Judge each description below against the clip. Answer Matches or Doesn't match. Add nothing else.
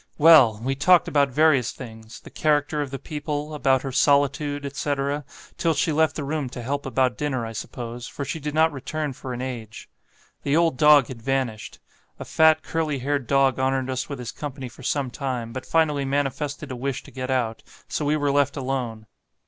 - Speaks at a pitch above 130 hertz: Matches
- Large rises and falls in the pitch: Doesn't match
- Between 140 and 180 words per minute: Doesn't match